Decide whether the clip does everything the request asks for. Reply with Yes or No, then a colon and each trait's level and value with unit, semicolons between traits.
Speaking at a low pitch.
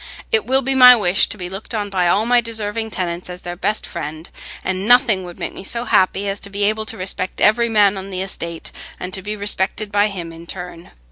No: high, 200 Hz